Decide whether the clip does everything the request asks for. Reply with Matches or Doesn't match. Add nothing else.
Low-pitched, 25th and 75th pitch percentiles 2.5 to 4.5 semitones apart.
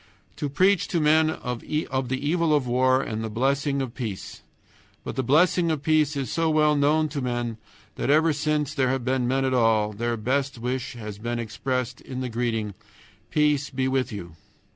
Matches